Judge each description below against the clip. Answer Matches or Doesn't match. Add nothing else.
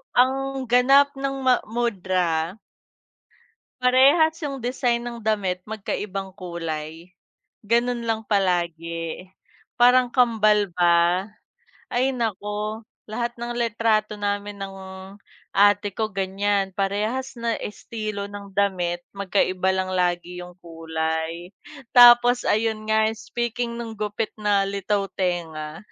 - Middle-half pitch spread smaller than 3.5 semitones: Doesn't match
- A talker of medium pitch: Doesn't match